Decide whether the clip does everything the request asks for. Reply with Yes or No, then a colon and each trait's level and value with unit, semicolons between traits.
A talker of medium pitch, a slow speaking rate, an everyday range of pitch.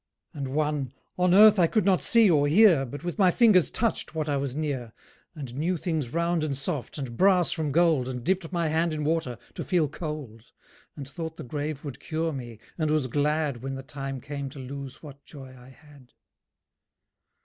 No: medium, 150 Hz; average, 200 wpm; average, 3.6 semitones